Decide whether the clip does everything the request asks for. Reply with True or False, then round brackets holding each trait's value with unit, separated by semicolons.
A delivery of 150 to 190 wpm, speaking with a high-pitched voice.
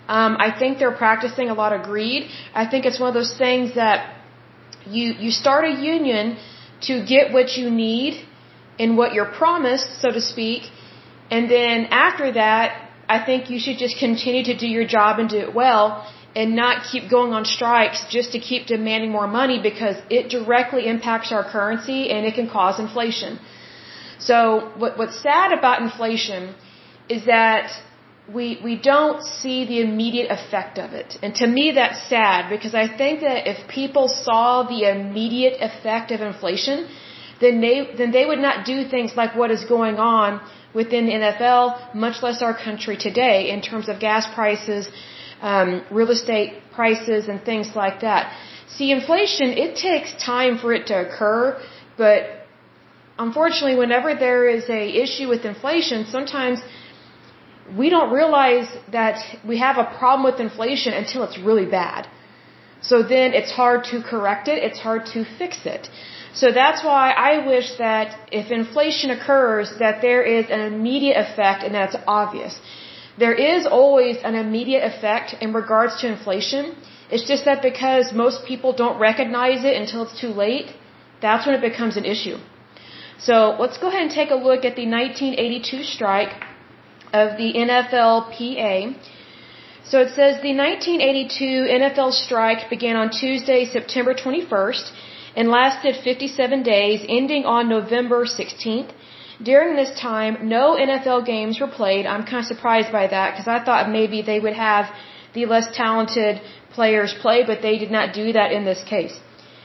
True (165 wpm; 235 Hz)